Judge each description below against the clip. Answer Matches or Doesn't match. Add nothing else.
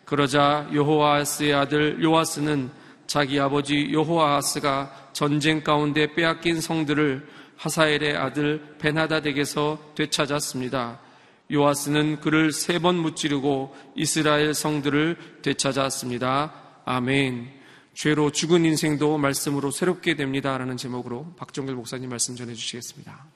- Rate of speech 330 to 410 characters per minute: Doesn't match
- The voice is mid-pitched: Matches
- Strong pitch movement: Doesn't match